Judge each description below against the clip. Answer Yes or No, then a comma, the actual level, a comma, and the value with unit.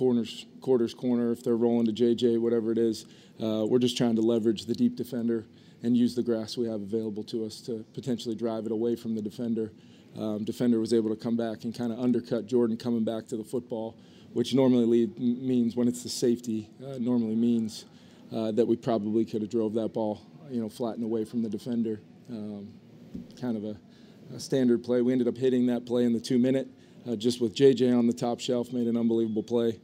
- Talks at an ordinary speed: No, fast, 220 wpm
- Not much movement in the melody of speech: Yes, narrow, 1.4 semitones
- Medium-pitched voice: No, low, 115 Hz